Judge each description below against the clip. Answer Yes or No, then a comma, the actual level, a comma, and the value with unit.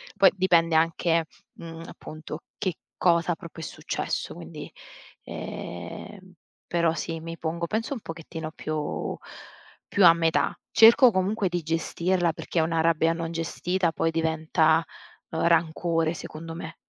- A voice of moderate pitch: Yes, medium, 165 Hz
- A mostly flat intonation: Yes, narrow, 1.5 semitones